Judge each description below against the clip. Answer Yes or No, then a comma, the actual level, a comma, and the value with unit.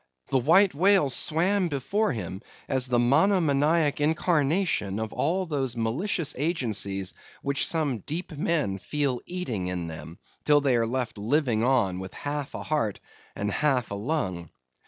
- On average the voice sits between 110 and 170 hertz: Yes, medium, 140 Hz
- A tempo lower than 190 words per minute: Yes, average, 150 wpm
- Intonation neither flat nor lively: No, wide, 6.3 semitones